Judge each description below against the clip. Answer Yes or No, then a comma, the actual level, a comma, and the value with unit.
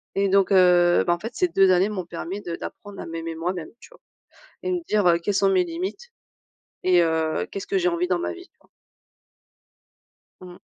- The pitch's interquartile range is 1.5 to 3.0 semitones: Yes, narrow, 2.4 semitones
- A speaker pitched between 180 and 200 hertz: Yes, medium, 185 Hz